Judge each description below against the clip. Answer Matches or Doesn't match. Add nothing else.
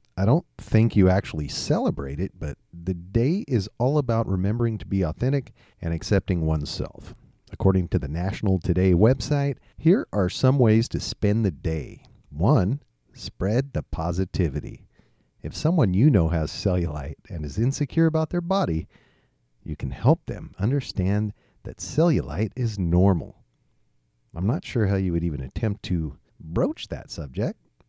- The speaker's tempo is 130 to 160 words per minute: Matches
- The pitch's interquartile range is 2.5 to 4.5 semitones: Doesn't match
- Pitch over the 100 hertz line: Doesn't match